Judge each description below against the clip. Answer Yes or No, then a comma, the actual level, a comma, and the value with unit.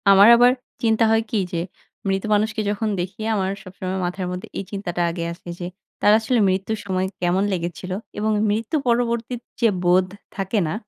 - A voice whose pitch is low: No, high, 195 Hz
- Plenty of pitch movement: No, average, 3.2 semitones